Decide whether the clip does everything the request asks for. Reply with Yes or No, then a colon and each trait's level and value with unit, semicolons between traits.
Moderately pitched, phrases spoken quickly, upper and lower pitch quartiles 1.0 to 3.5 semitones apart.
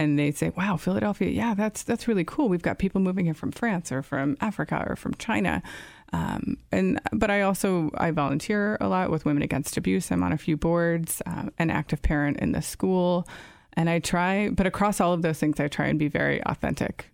No: medium, 170 Hz; fast, 220 wpm; average, 4.7 semitones